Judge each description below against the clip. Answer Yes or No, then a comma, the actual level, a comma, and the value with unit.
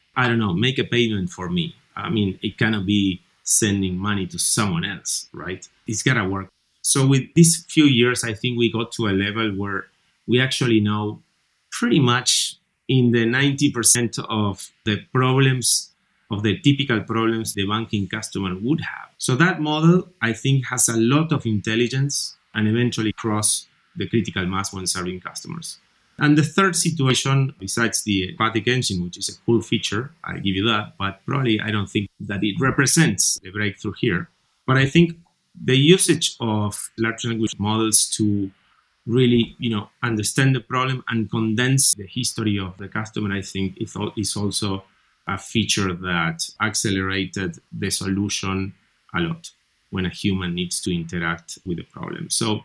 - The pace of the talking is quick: No, average, 170 wpm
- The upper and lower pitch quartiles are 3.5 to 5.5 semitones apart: Yes, average, 4.5 semitones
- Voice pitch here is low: Yes, low, 110 Hz